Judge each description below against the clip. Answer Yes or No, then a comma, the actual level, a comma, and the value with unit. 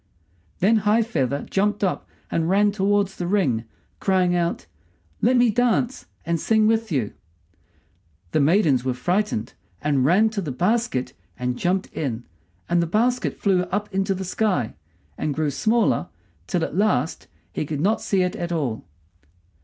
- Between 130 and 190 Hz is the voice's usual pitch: Yes, medium, 185 Hz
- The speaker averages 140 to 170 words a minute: Yes, average, 160 wpm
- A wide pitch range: Yes, wide, 5.7 semitones